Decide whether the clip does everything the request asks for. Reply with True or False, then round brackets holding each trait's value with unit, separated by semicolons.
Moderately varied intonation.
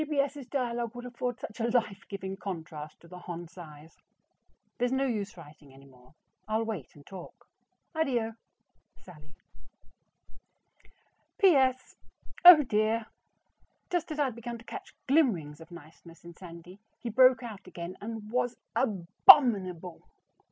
False (6.5 semitones)